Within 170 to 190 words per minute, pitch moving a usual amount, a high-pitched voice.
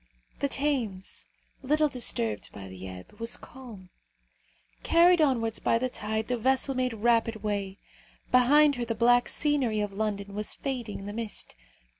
No: average, 155 wpm; average, 4.2 semitones; high, 230 Hz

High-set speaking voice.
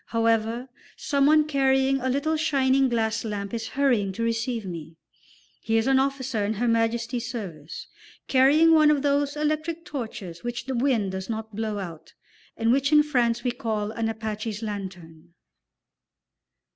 Yes: high, 235 Hz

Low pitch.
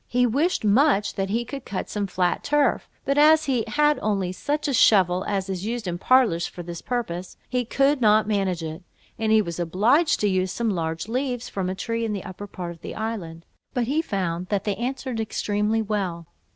No: high, 210 Hz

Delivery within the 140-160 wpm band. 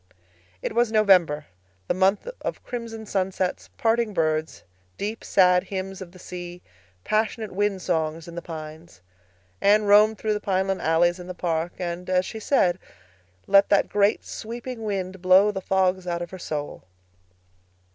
Yes: average, 155 wpm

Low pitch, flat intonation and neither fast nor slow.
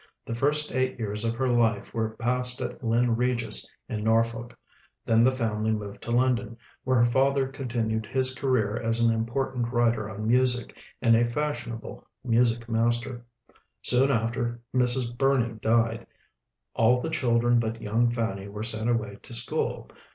Yes: low, 120 Hz; narrow, 1.7 semitones; average, 160 wpm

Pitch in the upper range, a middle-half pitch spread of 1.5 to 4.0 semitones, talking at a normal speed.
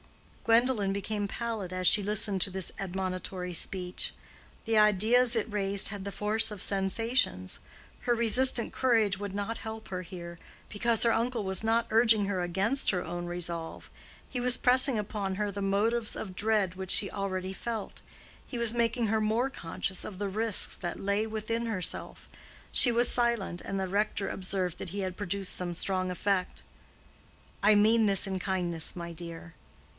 Yes: high, 200 Hz; average, 3.3 semitones; average, 170 wpm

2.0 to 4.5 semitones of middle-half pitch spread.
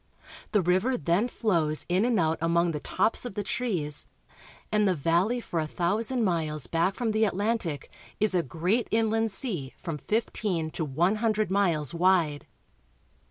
No: average, 4.9 semitones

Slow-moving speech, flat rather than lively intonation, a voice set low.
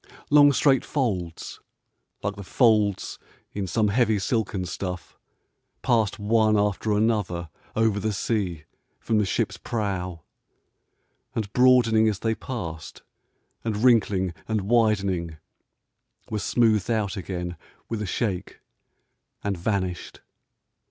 No: slow, 115 wpm; average, 3.2 semitones; low, 105 Hz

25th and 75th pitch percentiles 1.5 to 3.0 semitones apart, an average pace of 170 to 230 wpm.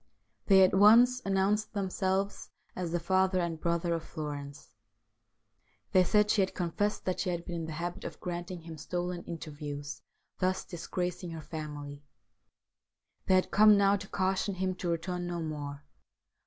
No: average, 2.7 semitones; average, 160 wpm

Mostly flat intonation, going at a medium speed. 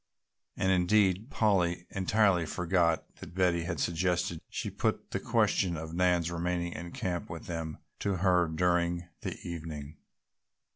Yes: narrow, 1.5 semitones; average, 145 wpm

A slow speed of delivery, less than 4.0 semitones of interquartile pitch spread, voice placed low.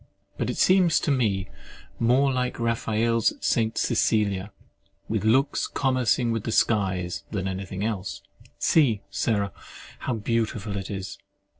Yes: slow, 125 wpm; average, 3.4 semitones; low, 110 Hz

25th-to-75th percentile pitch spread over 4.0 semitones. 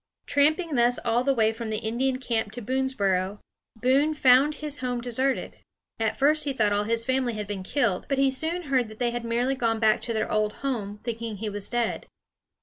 No: average, 3.4 semitones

